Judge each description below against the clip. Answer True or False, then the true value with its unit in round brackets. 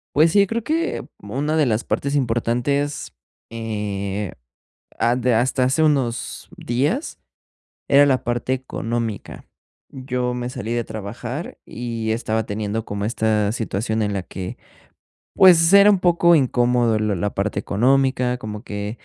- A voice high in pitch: False (120 Hz)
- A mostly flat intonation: False (4.2 semitones)